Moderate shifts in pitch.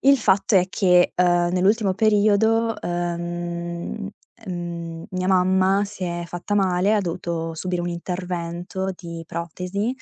No: narrow, 2.3 semitones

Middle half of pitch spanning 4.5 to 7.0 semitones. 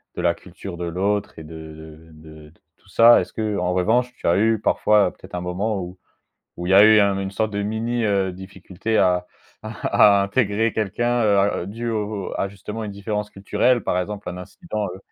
No: average, 3.3 semitones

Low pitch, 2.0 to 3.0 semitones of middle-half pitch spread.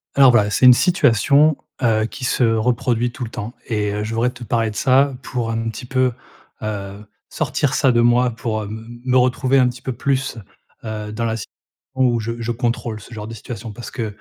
Yes: low, 120 Hz; narrow, 2.6 semitones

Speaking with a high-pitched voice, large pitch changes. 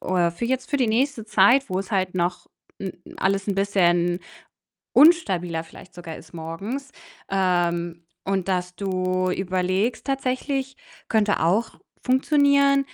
Yes: high, 195 Hz; wide, 6.0 semitones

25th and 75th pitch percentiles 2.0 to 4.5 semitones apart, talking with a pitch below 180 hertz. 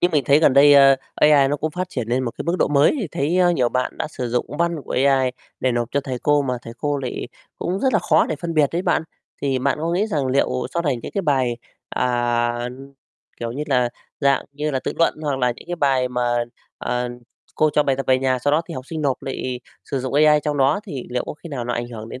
Yes: average, 3.3 semitones; medium, 140 Hz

